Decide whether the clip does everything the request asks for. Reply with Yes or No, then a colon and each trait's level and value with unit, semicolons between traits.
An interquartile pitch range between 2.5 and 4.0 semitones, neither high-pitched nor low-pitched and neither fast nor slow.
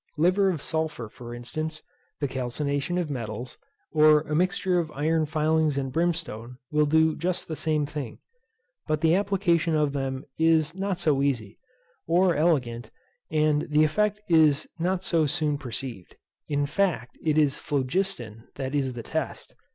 Yes: average, 3.4 semitones; medium, 155 Hz; average, 155 wpm